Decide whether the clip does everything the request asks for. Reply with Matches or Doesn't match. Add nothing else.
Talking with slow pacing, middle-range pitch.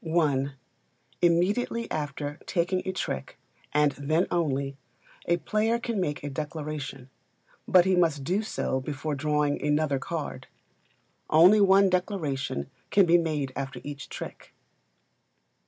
Matches